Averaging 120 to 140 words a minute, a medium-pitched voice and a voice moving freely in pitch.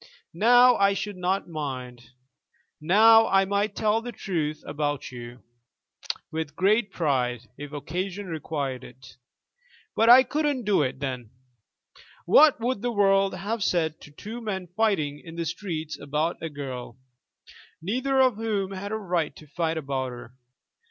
No: average, 150 wpm; medium, 175 Hz; wide, 6.4 semitones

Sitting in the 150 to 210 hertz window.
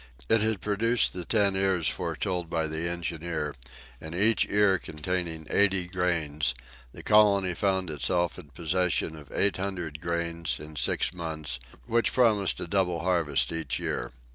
No: very low, 90 Hz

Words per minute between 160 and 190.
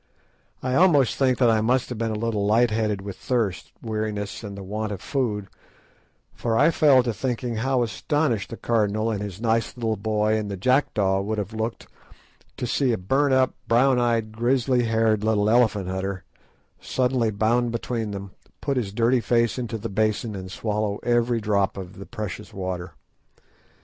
Yes: average, 180 wpm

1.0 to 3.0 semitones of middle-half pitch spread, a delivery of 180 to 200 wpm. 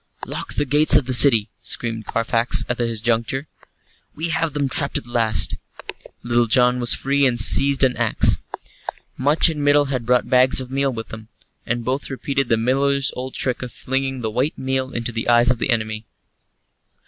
Yes: average, 2.7 semitones; average, 190 wpm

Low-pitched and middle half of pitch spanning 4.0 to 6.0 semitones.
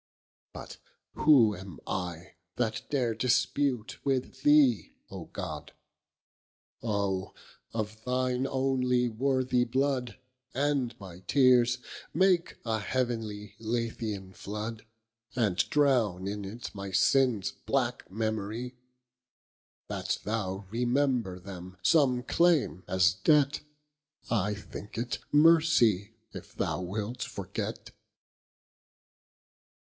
Yes: low, 115 Hz; average, 4.3 semitones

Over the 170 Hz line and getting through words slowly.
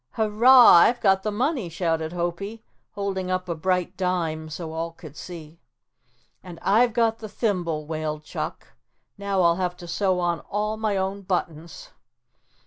No: medium, 185 Hz; average, 155 wpm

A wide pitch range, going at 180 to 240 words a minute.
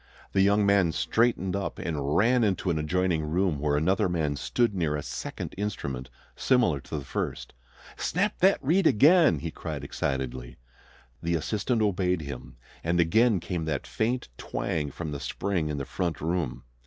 No: wide, 5.7 semitones; average, 165 wpm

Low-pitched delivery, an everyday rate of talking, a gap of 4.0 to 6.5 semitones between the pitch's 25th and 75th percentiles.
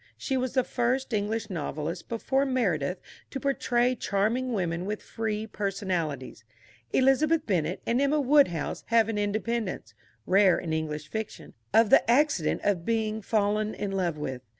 No: high, 215 Hz; average, 150 wpm; average, 5.2 semitones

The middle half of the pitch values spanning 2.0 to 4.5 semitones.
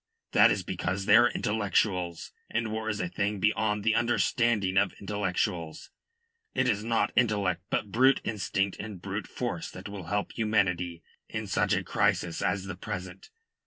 Yes: average, 3.0 semitones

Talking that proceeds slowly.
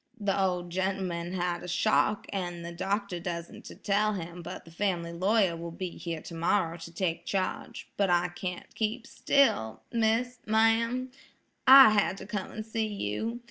No: average, 155 wpm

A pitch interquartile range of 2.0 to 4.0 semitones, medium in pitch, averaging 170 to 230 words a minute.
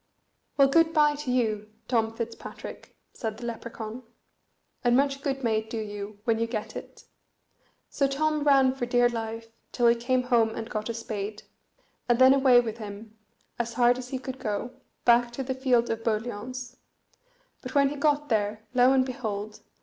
No: average, 2.8 semitones; high, 240 Hz; average, 180 wpm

